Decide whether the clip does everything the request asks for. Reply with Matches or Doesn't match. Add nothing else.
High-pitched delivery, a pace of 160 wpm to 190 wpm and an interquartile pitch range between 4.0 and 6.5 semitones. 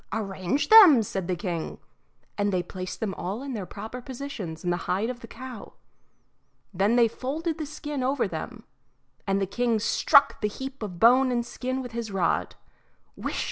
Matches